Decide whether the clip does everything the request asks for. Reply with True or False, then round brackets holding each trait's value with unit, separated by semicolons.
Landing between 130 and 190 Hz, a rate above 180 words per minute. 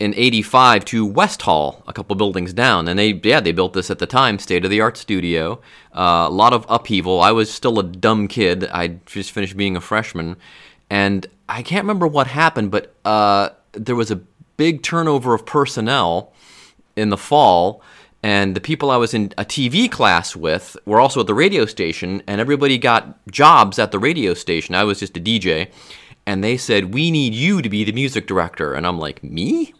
False (105 Hz; 205 wpm)